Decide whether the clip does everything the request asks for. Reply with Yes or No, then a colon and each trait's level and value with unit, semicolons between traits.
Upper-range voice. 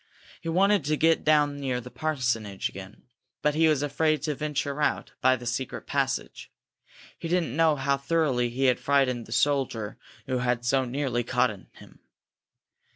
No: medium, 140 Hz